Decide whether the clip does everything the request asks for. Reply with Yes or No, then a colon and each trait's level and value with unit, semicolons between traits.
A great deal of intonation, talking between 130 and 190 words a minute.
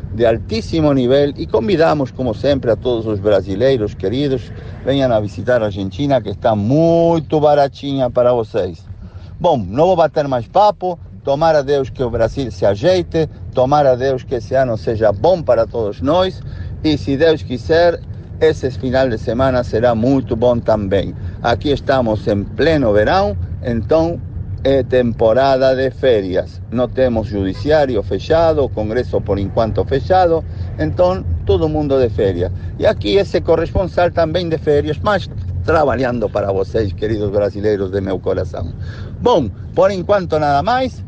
Yes: wide, 5.8 semitones; average, 155 wpm